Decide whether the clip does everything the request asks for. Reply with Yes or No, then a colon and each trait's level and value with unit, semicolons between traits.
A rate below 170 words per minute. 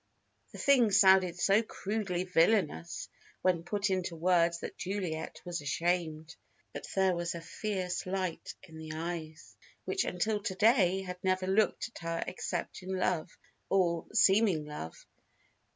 Yes: average, 145 wpm